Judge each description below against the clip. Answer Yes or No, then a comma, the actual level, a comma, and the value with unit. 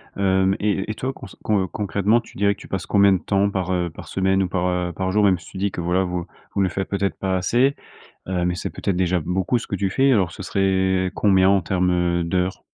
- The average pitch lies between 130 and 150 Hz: No, very low, 95 Hz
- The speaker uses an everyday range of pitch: No, narrow, 1.7 semitones